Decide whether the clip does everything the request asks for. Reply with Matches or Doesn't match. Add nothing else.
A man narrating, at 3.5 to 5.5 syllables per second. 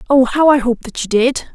Doesn't match